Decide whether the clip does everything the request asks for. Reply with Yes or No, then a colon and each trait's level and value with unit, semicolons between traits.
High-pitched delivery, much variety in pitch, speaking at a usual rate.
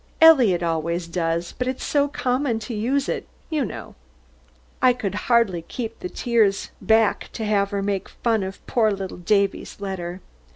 No: high, 210 Hz; average, 4.4 semitones; average, 165 wpm